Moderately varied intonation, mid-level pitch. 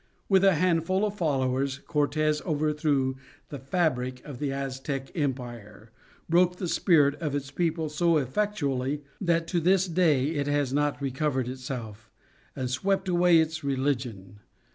Yes: average, 4.2 semitones; medium, 145 Hz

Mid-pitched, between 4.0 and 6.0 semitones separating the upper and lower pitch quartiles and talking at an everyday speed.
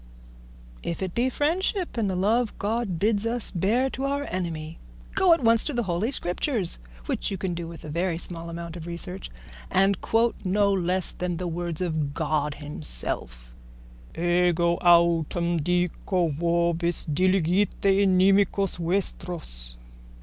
No: medium, 180 Hz; average, 3.1 semitones; average, 150 wpm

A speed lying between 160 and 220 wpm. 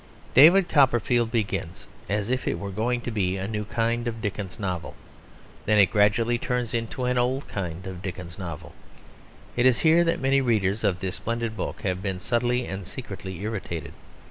Yes: average, 180 wpm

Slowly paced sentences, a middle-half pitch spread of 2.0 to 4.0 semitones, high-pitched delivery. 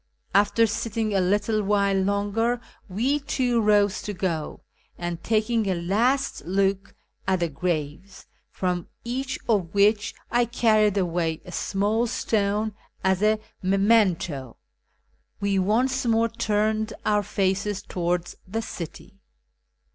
Yes: slow, 125 wpm; average, 3.1 semitones; high, 205 Hz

